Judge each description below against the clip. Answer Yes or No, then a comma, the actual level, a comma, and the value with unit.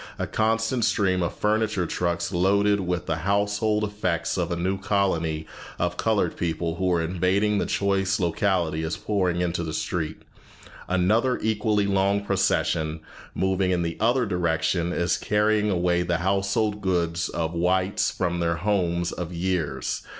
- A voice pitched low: Yes, very low, 95 Hz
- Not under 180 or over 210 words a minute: No, average, 155 wpm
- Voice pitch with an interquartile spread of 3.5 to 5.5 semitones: No, average, 3.0 semitones